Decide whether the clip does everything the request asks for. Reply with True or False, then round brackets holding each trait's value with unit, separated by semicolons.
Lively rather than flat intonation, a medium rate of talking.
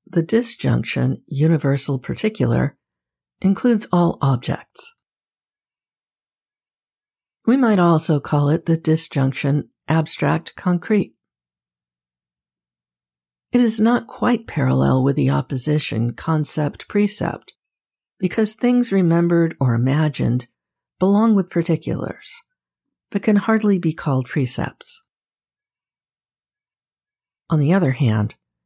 False (8.4 semitones; 90 wpm)